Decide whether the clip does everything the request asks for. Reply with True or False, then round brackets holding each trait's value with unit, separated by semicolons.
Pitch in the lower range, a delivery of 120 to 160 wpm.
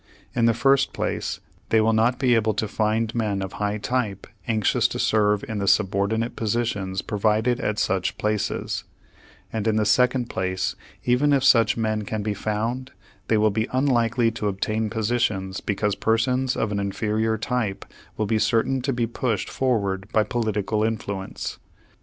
False (110 Hz; 170 wpm)